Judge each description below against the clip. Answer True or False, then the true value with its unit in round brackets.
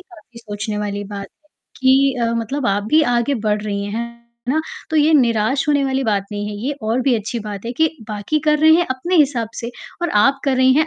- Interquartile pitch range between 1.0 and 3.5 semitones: False (4.7 semitones)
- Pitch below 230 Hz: False (240 Hz)